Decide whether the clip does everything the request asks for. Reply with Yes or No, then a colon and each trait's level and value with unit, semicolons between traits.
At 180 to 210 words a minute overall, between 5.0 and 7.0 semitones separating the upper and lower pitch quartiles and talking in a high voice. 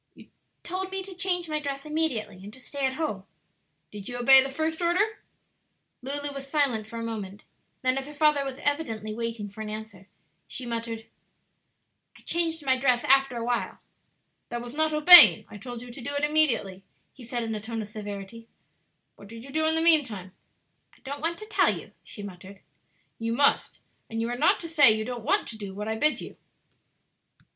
Yes: fast, 205 wpm; wide, 5.6 semitones; very high, 250 Hz